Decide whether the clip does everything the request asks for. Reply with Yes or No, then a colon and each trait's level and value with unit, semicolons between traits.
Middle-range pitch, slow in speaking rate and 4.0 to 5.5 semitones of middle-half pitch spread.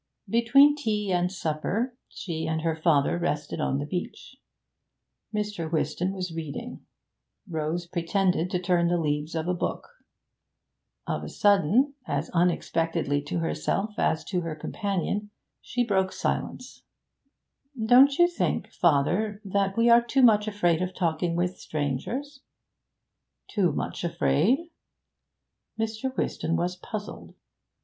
Yes: medium, 180 Hz; slow, 130 wpm; average, 4.6 semitones